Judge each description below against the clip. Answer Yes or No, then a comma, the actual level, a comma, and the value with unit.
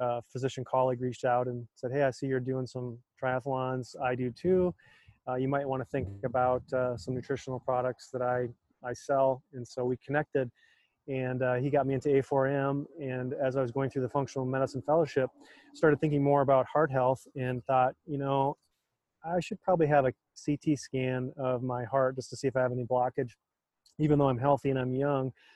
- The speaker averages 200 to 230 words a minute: Yes, fast, 205 wpm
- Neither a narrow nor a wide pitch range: No, narrow, 1.7 semitones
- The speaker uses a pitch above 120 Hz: Yes, low, 130 Hz